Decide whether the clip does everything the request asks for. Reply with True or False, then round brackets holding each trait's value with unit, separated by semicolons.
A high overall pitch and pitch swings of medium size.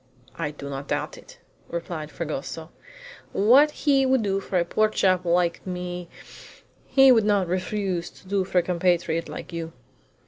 False (180 Hz; 3.2 semitones)